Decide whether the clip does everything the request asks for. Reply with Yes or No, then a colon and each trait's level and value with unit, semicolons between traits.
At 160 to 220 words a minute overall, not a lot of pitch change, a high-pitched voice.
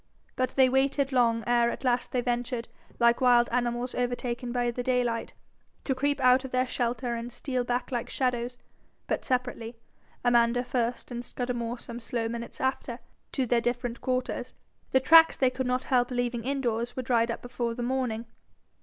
Yes: average, 180 wpm; narrow, 1.2 semitones; high, 245 Hz